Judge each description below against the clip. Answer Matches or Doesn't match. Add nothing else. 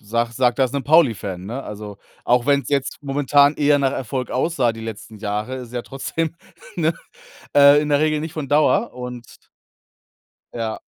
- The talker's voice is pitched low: Matches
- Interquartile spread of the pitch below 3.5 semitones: Doesn't match